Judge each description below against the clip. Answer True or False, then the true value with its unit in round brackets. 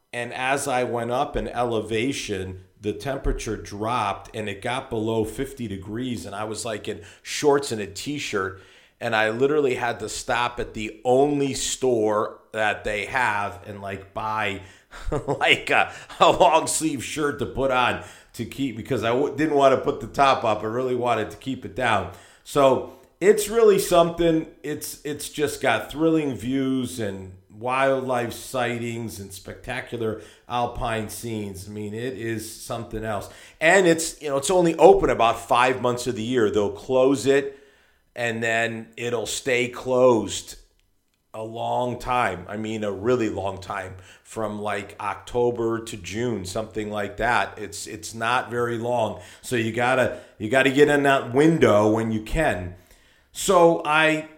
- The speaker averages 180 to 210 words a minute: False (165 wpm)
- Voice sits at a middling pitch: False (120 Hz)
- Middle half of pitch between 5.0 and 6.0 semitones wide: False (3.9 semitones)